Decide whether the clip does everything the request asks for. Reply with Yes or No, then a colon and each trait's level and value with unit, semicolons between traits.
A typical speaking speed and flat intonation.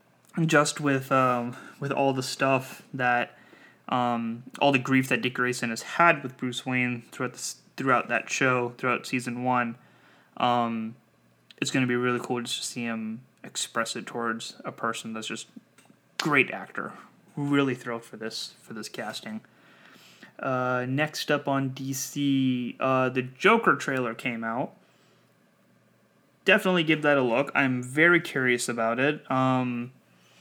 Yes: average, 150 wpm; narrow, 2.0 semitones